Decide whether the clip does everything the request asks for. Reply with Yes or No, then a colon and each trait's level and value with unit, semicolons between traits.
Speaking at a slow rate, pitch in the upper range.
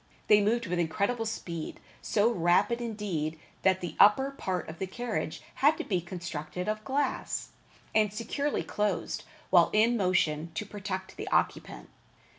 No: average, 150 wpm; high, 205 Hz